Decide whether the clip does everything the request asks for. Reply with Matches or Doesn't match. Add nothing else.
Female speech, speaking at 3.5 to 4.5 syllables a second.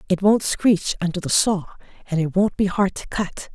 Doesn't match